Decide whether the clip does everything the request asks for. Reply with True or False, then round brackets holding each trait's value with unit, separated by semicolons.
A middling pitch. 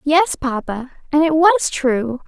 False (285 Hz)